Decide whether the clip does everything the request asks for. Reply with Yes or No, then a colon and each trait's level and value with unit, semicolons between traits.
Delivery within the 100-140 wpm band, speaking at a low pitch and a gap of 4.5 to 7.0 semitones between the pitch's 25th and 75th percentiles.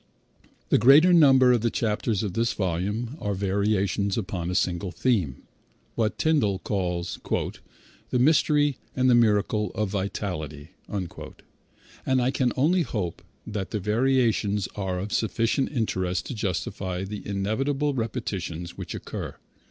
Yes: slow, 135 wpm; low, 105 Hz; average, 4.9 semitones